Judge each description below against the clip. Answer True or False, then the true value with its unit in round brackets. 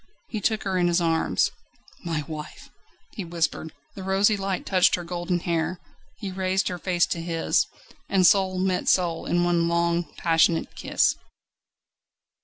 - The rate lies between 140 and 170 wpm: True (155 wpm)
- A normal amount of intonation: False (1.9 semitones)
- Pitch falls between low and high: True (175 Hz)